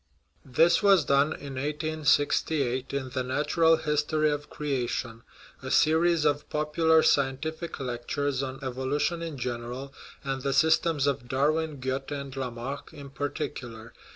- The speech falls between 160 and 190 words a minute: No, slow, 135 wpm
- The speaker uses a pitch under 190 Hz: Yes, medium, 140 Hz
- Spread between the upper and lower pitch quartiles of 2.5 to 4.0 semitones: Yes, average, 2.8 semitones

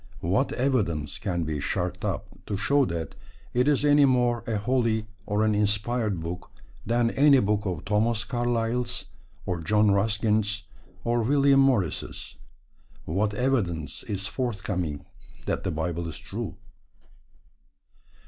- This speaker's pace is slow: Yes, slow, 130 wpm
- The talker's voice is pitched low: Yes, low, 105 Hz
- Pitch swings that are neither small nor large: Yes, average, 4.5 semitones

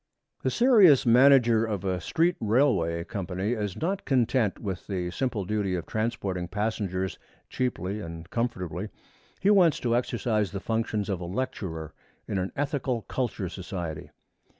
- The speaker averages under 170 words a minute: Yes, average, 145 wpm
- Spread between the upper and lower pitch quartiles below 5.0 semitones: No, average, 5.3 semitones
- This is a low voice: Yes, low, 105 Hz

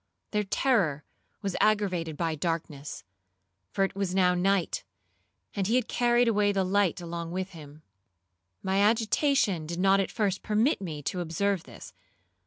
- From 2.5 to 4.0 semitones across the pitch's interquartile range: Yes, average, 3.6 semitones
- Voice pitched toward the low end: No, high, 190 Hz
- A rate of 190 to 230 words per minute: No, average, 155 wpm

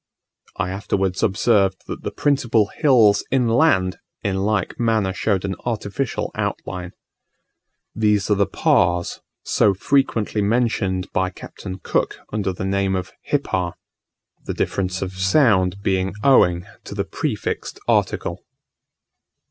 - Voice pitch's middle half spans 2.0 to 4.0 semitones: Yes, average, 3.3 semitones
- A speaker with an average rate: No, slow, 125 wpm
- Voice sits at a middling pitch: No, low, 100 Hz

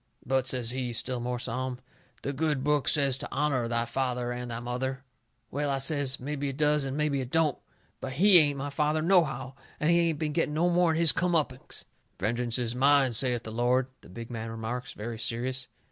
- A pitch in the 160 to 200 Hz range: No, low, 130 Hz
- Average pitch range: Yes, average, 3.3 semitones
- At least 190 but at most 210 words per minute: Yes, fast, 205 wpm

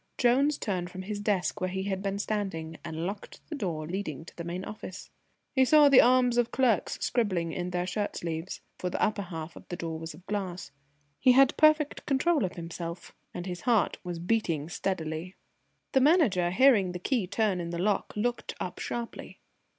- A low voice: No, high, 190 Hz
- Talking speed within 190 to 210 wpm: Yes, average, 195 wpm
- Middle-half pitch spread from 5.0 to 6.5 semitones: Yes, wide, 5.4 semitones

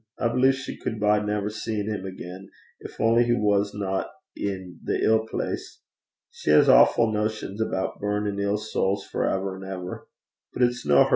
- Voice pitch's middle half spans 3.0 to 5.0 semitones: No, narrow, 2.4 semitones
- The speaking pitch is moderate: No, low, 105 Hz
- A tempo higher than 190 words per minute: No, average, 180 wpm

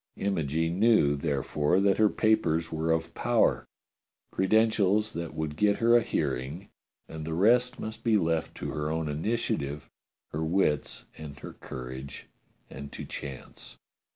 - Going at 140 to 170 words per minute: Yes, average, 150 wpm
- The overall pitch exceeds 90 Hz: No, very low, 80 Hz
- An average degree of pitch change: No, wide, 5.9 semitones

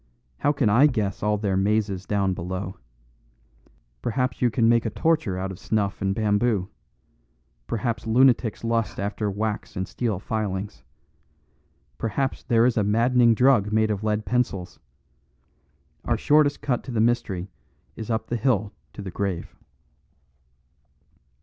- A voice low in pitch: Yes, low, 110 Hz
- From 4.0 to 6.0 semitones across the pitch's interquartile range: No, average, 3.2 semitones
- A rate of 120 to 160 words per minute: Yes, average, 145 wpm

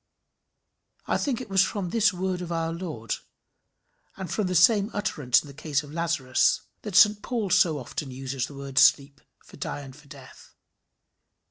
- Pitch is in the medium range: Yes, medium, 165 Hz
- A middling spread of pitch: No, wide, 5.7 semitones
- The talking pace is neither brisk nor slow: Yes, average, 175 wpm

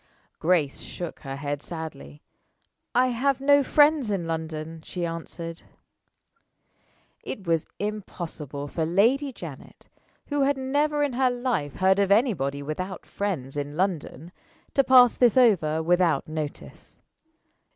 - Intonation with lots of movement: Yes, wide, 8.0 semitones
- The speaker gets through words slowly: Yes, slow, 130 wpm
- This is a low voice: No, medium, 180 Hz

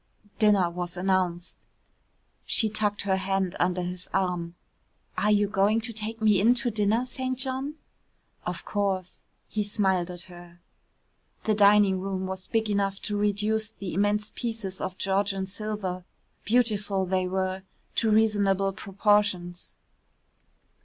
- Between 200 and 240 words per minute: No, slow, 135 wpm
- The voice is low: No, high, 200 Hz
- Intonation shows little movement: Yes, narrow, 2.2 semitones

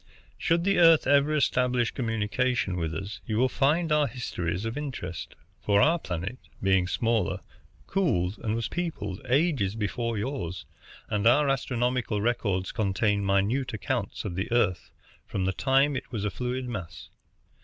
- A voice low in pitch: Yes, low, 115 Hz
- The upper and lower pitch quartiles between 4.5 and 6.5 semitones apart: Yes, wide, 5.4 semitones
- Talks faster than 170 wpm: No, average, 155 wpm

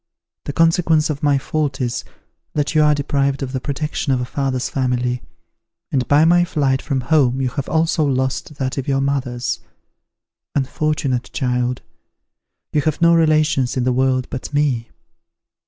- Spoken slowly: No, average, 160 wpm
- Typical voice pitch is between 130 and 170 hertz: Yes, medium, 140 Hz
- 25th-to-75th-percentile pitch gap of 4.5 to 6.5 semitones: No, average, 2.8 semitones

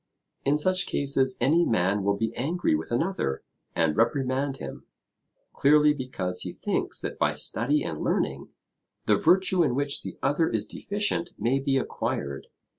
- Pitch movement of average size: No, wide, 5.8 semitones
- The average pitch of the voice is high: No, low, 135 Hz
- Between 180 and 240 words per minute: No, average, 155 wpm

